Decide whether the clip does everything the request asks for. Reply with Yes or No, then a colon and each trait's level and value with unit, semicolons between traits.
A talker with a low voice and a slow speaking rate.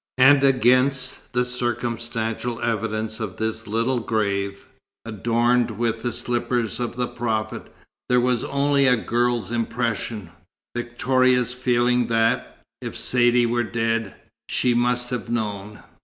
Yes: low, 120 Hz; slow, 125 wpm